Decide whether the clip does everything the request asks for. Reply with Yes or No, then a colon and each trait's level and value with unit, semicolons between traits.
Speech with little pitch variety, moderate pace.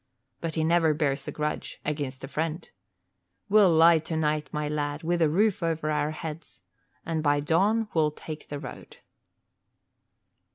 Yes: narrow, 1.8 semitones; average, 155 wpm